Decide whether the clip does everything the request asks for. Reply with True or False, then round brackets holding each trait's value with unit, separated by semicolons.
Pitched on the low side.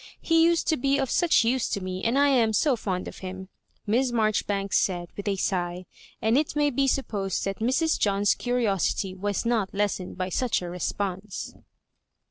False (210 Hz)